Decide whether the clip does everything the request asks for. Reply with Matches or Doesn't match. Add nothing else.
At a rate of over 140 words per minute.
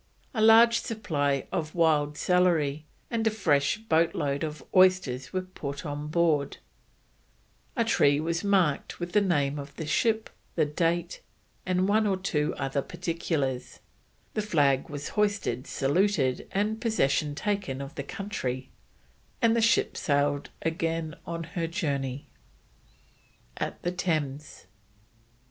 Doesn't match